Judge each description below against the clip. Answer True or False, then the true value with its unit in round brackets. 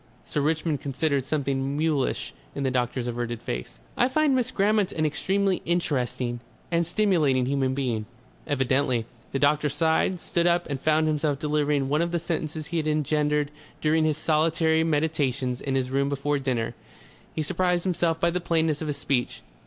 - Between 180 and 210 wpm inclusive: False (170 wpm)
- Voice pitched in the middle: True (150 Hz)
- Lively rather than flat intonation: False (3.2 semitones)